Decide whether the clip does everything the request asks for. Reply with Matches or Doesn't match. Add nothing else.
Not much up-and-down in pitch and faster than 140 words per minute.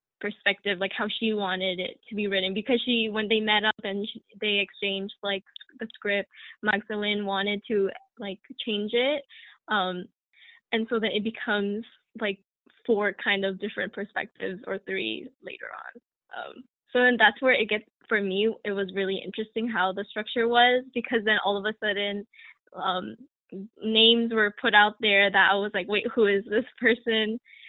Matches